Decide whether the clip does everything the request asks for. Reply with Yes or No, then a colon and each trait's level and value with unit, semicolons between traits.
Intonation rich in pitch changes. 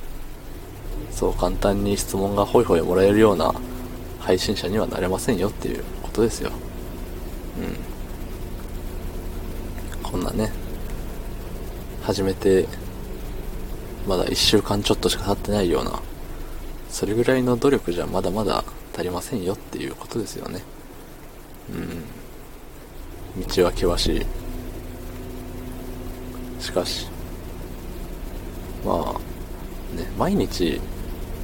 No: average, 2.7 semitones